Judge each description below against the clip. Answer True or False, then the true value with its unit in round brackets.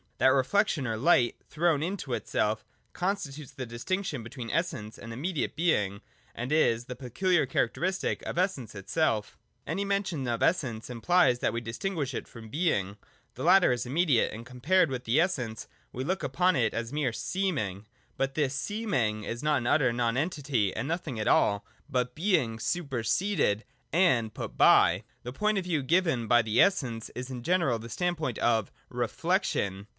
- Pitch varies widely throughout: True (7.0 semitones)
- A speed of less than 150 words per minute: False (170 wpm)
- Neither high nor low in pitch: False (130 Hz)